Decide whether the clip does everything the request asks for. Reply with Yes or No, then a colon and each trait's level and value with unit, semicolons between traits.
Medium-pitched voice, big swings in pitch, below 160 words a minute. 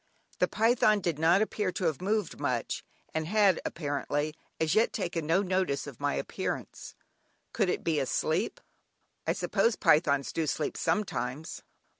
No: medium, 165 Hz; average, 4.9 semitones; average, 150 wpm